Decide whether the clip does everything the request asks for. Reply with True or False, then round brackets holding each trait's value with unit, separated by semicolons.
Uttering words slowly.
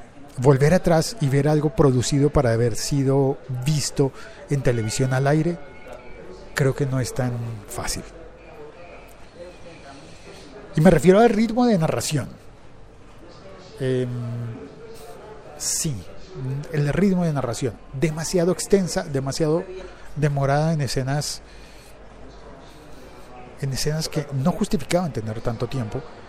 True (105 wpm)